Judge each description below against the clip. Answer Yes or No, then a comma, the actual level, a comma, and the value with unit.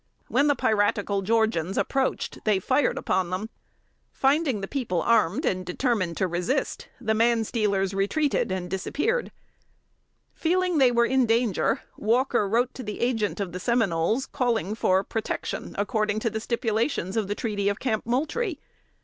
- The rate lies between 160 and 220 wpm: No, average, 150 wpm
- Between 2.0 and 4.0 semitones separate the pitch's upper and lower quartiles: No, average, 4.5 semitones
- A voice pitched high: Yes, high, 220 Hz